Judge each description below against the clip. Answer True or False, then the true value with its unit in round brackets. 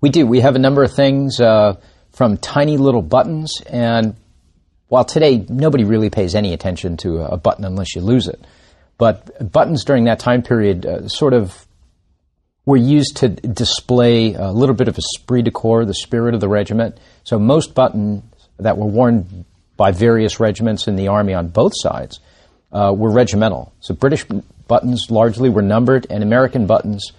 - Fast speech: False (180 wpm)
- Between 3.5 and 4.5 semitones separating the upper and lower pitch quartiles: True (3.9 semitones)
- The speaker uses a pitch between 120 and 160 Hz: False (110 Hz)